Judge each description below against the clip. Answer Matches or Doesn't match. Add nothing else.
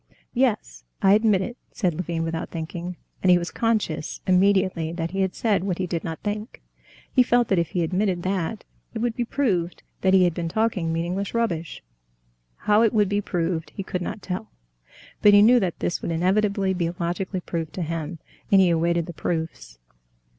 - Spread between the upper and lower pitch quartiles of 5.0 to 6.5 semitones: Doesn't match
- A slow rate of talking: Doesn't match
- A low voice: Doesn't match